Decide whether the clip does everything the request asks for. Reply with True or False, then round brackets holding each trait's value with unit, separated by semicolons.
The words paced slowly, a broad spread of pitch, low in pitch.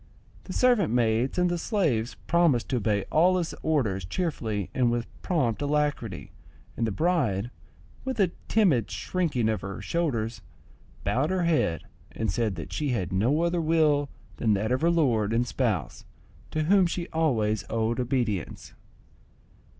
False (155 wpm; 7.1 semitones; 125 Hz)